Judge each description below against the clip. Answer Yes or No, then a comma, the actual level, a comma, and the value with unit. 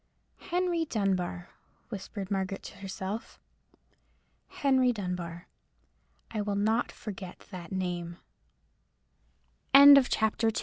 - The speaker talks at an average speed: No, slow, 85 wpm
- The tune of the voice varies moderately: Yes, average, 3.5 semitones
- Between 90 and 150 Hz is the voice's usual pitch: No, high, 200 Hz